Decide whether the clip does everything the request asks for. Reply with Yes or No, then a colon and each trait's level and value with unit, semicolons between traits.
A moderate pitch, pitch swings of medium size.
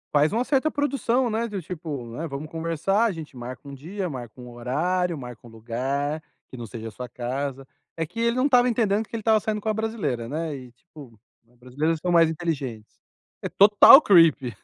No: medium, 160 Hz; wide, 8.5 semitones